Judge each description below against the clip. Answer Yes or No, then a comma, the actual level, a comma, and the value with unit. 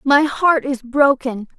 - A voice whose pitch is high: Yes, very high, 270 Hz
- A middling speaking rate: Yes, average, 150 wpm